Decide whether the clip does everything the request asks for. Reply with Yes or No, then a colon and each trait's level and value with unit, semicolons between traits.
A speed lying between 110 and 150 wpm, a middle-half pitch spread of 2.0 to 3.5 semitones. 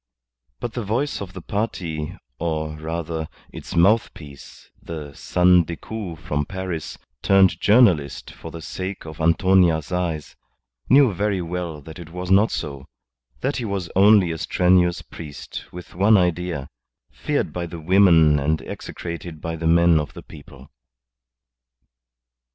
Yes: average, 140 wpm; average, 3.2 semitones